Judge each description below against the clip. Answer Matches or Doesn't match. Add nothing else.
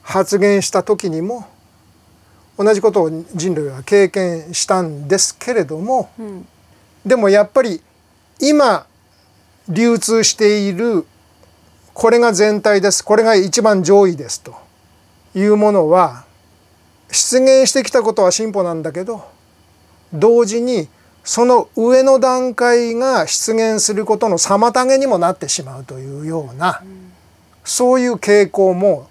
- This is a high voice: Matches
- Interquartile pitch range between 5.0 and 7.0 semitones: Doesn't match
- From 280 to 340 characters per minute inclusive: Doesn't match